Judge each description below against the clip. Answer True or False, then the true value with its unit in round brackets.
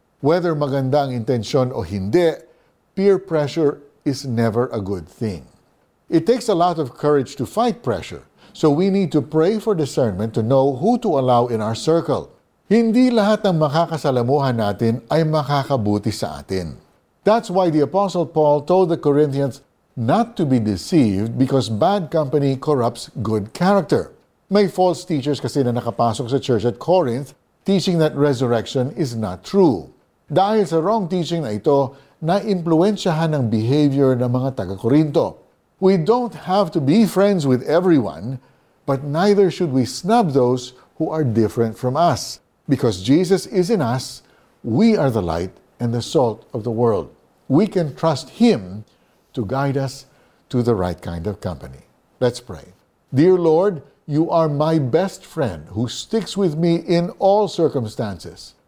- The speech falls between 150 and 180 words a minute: True (155 wpm)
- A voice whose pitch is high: False (145 Hz)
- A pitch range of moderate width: False (6.6 semitones)